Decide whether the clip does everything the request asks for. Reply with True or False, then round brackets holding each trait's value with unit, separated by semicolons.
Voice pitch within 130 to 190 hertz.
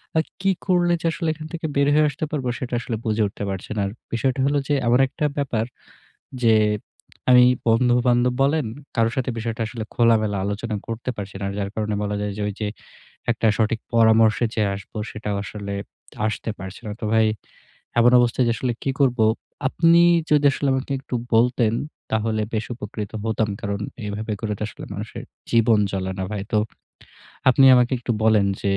False (115 Hz)